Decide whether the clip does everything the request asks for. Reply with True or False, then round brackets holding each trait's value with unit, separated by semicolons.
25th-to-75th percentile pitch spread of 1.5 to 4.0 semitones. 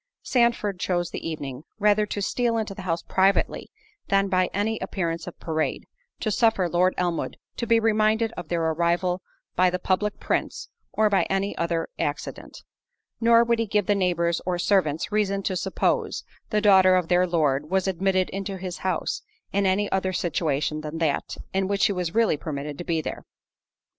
True (3.3 semitones)